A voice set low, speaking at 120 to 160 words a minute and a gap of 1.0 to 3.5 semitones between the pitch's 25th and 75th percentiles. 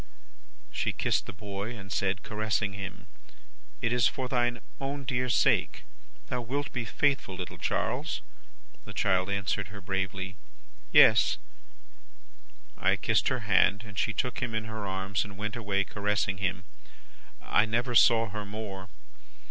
Yes: low, 105 Hz; average, 150 wpm; average, 3.2 semitones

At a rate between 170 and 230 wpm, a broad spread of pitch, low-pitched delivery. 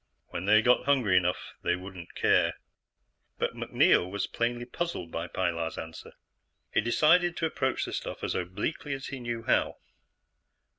No: average, 155 wpm; wide, 6.8 semitones; low, 115 Hz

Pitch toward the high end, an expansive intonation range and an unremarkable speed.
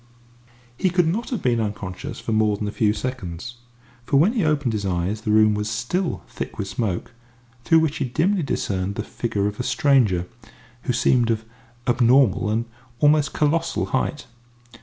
No: low, 120 Hz; wide, 6.0 semitones; average, 175 wpm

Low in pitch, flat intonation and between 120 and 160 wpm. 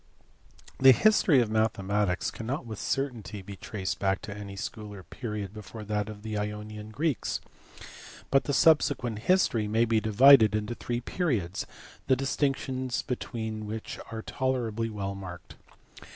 No: low, 110 Hz; average, 3.5 semitones; average, 145 wpm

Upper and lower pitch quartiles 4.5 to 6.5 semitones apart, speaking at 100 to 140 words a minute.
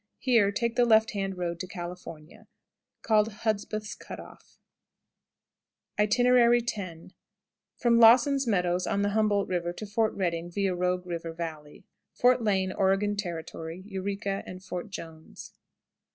No: average, 3.7 semitones; slow, 135 wpm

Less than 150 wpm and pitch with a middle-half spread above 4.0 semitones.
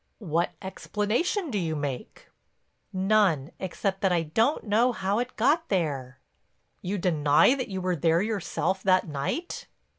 Yes: average, 140 wpm; average, 4.9 semitones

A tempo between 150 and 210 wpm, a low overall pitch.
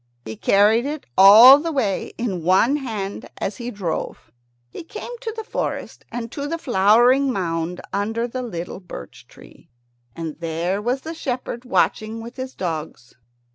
No: average, 160 wpm; high, 225 Hz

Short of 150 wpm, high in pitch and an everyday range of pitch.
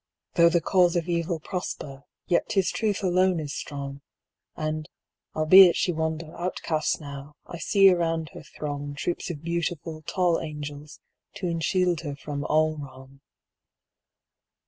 No: average, 140 wpm; medium, 160 Hz; average, 3.0 semitones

